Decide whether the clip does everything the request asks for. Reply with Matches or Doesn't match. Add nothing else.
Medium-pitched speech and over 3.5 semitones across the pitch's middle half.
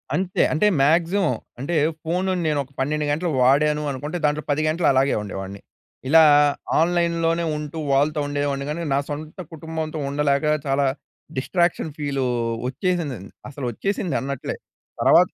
Doesn't match